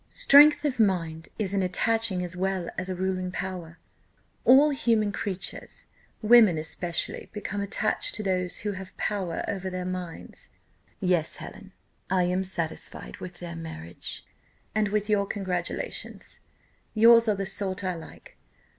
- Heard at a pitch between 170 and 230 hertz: Yes, high, 190 Hz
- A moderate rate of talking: Yes, average, 145 wpm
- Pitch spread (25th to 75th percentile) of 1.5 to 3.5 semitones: Yes, average, 2.7 semitones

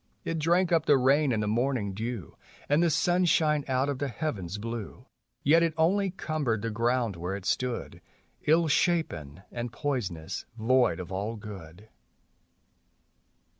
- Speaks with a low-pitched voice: Yes, low, 125 Hz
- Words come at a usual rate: Yes, average, 150 wpm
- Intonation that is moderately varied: No, wide, 6.9 semitones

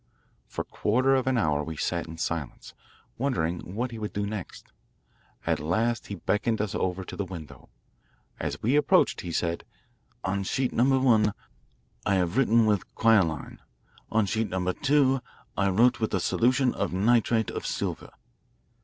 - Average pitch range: Yes, average, 4.9 semitones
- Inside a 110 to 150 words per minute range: No, average, 165 wpm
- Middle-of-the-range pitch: No, low, 105 Hz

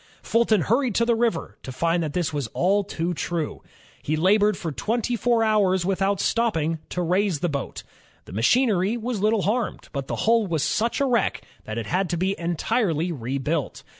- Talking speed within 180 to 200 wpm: Yes, average, 190 wpm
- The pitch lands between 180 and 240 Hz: Yes, medium, 185 Hz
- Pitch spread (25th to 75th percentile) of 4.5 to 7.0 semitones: Yes, wide, 5.5 semitones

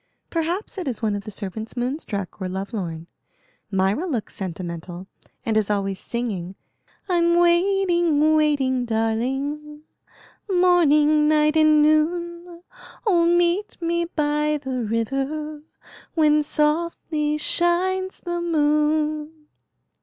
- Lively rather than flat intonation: Yes, wide, 6.8 semitones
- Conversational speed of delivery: No, slow, 115 wpm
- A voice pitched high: Yes, very high, 300 Hz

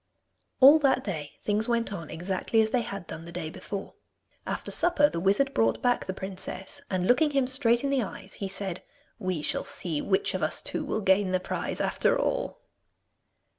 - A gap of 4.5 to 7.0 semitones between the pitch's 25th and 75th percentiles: Yes, average, 5.3 semitones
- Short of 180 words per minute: No, average, 195 wpm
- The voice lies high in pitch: Yes, high, 200 Hz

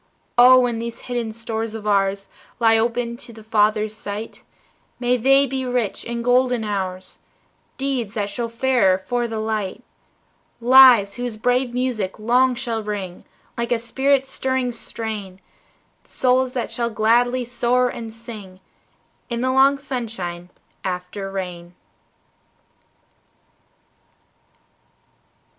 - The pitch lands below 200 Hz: No, high, 235 Hz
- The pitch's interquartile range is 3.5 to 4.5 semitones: No, average, 2.9 semitones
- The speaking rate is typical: No, slow, 120 wpm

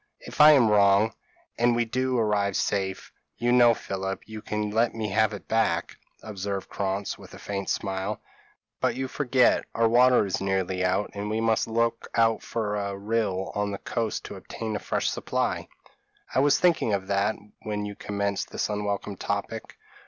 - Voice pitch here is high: No, low, 105 Hz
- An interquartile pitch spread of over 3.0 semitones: No, narrow, 2.4 semitones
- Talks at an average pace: Yes, average, 180 wpm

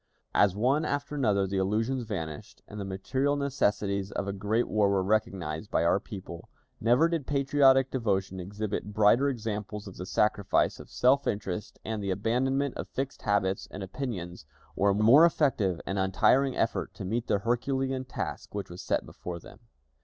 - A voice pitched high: No, low, 105 Hz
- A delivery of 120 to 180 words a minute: Yes, average, 170 wpm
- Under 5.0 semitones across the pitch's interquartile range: No, average, 5.3 semitones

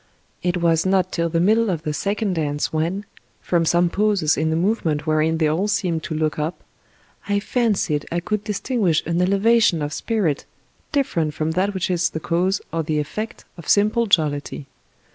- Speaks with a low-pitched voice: No, medium, 175 Hz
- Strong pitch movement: No, average, 4.3 semitones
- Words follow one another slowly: No, average, 180 wpm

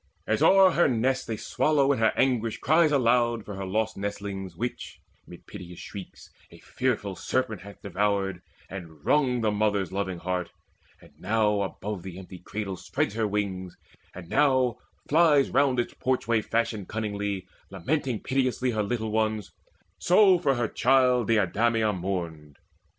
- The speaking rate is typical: Yes, average, 150 wpm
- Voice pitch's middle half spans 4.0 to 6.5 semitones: Yes, average, 4.6 semitones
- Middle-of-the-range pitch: No, low, 110 Hz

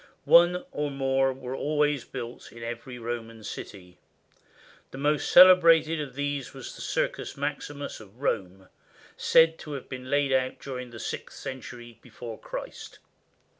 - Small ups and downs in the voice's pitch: No, average, 3.6 semitones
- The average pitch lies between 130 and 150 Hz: Yes, low, 135 Hz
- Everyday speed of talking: Yes, average, 150 wpm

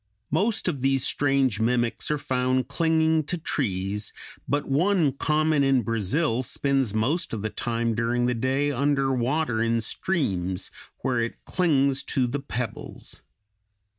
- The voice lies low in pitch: Yes, low, 130 Hz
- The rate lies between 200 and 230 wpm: No, average, 140 wpm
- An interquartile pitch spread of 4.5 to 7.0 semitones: No, average, 4.0 semitones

